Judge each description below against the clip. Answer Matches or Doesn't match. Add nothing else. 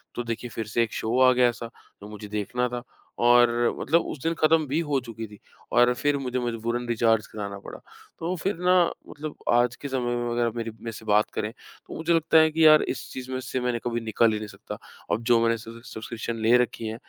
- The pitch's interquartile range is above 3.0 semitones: Doesn't match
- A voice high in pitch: Doesn't match